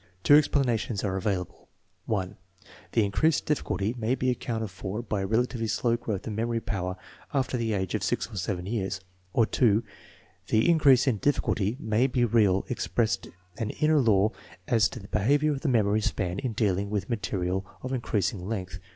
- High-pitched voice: No, low, 110 Hz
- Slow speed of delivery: No, average, 175 wpm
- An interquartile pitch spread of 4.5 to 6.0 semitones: No, average, 3.8 semitones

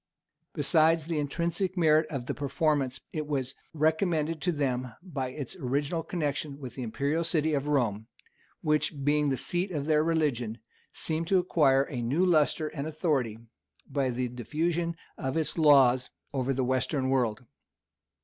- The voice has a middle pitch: Yes, medium, 145 Hz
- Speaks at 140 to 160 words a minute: Yes, average, 155 wpm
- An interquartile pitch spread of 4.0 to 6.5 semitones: No, average, 3.5 semitones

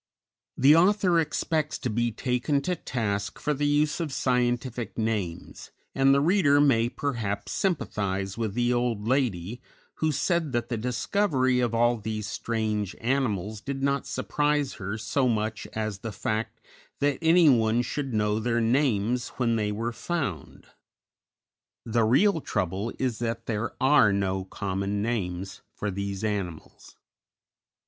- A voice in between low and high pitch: No, low, 120 Hz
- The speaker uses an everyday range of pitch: Yes, average, 4.7 semitones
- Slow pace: No, average, 145 wpm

